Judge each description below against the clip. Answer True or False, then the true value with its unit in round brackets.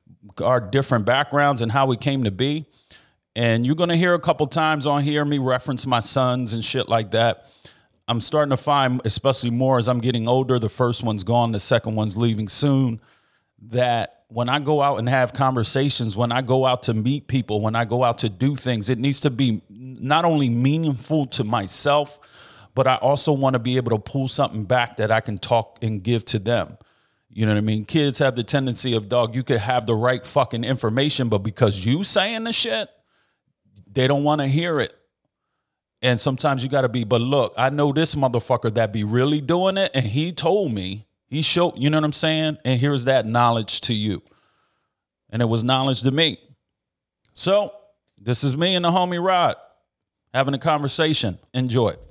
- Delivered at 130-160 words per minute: False (205 wpm)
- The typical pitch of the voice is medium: False (130 Hz)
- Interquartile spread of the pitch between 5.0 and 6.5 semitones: False (3.7 semitones)